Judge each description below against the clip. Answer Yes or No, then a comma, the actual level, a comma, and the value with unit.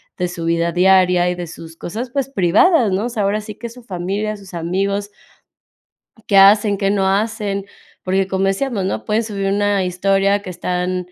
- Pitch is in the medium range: No, high, 195 Hz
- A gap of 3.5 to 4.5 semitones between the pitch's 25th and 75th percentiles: No, narrow, 2.5 semitones